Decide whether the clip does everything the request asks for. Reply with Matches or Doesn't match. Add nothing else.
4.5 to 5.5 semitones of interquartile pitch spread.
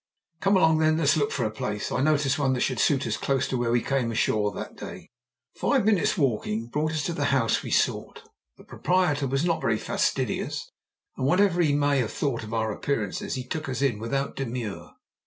Matches